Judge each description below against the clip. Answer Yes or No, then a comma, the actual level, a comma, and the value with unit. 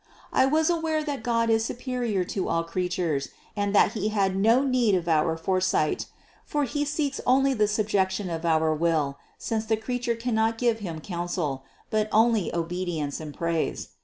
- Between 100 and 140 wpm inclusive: No, average, 180 wpm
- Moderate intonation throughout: No, wide, 5.9 semitones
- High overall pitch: Yes, high, 205 Hz